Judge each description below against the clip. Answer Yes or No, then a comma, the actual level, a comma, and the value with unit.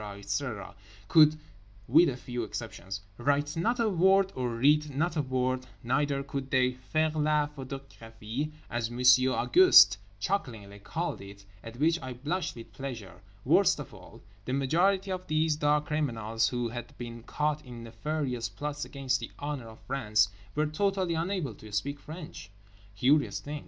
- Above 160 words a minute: No, average, 155 wpm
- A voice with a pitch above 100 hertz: Yes, low, 135 Hz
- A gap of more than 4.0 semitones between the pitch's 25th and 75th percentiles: Yes, average, 4.5 semitones